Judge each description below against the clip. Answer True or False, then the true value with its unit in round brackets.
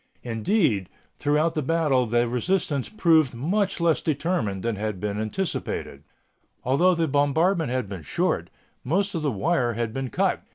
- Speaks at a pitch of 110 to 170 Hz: True (140 Hz)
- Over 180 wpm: False (155 wpm)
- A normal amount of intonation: False (6.3 semitones)